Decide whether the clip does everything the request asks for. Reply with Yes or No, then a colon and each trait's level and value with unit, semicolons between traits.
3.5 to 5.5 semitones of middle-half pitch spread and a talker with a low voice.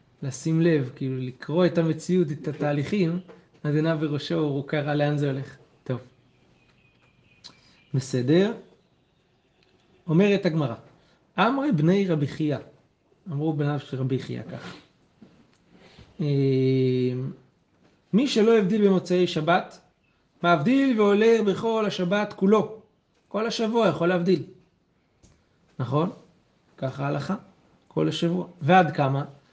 No: average, 4.9 semitones; medium, 165 Hz